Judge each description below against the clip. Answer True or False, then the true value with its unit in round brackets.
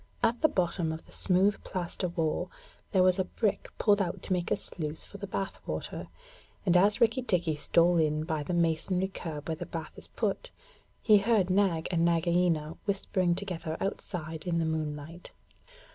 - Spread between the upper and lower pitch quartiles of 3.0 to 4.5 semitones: True (3.3 semitones)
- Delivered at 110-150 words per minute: False (180 wpm)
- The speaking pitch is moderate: True (175 Hz)